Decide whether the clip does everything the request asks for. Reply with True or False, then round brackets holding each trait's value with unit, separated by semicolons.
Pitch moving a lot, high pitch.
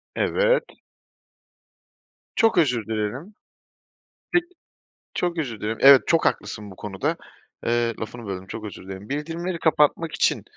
False (7.8 semitones; 125 Hz)